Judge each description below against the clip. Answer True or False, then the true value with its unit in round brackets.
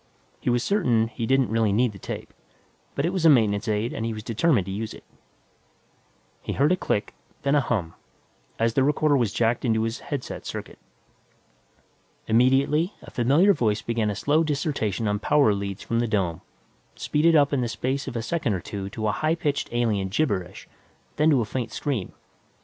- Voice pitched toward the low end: True (120 Hz)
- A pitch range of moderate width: True (5.0 semitones)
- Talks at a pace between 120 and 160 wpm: False (195 wpm)